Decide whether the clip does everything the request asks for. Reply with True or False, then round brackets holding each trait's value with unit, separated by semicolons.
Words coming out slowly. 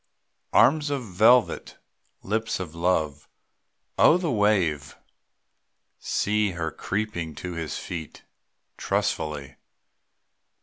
True (90 wpm)